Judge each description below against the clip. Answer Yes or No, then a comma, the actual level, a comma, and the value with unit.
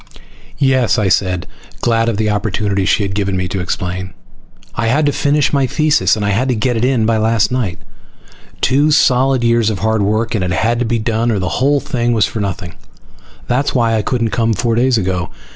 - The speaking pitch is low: Yes, low, 115 Hz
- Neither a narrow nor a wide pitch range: Yes, average, 3.8 semitones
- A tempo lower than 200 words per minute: No, fast, 205 wpm